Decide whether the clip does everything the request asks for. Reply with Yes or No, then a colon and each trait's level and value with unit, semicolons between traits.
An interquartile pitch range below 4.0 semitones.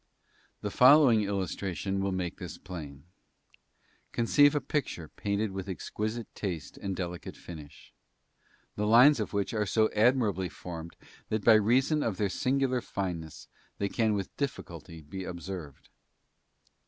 No: average, 4.5 semitones